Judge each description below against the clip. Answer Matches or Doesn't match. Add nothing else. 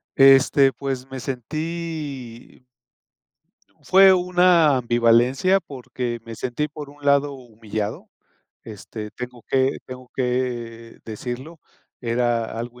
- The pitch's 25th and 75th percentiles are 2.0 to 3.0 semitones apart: Doesn't match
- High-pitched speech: Doesn't match